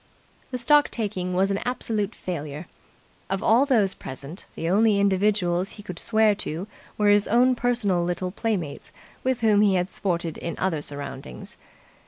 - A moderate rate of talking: Yes, average, 160 wpm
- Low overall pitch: No, high, 195 Hz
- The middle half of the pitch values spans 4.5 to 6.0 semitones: No, average, 3.9 semitones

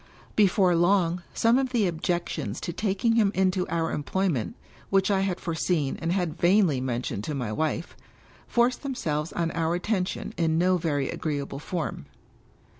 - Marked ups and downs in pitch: No, average, 3.7 semitones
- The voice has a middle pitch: Yes, medium, 175 Hz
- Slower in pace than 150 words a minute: No, average, 160 wpm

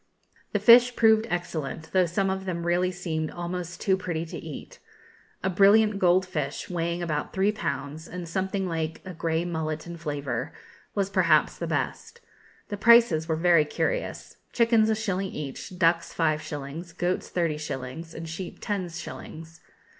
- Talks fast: No, average, 160 wpm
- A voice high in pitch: No, medium, 175 Hz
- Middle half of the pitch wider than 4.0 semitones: No, average, 3.1 semitones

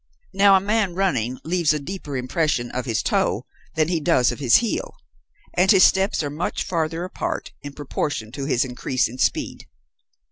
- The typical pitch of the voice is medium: Yes, medium, 150 Hz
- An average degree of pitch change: No, wide, 6.1 semitones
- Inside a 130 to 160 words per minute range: No, average, 180 wpm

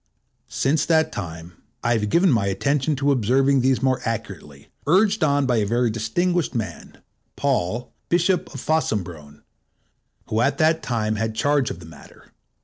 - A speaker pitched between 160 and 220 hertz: No, low, 125 Hz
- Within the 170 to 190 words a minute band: No, average, 155 wpm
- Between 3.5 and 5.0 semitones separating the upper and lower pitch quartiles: No, wide, 5.4 semitones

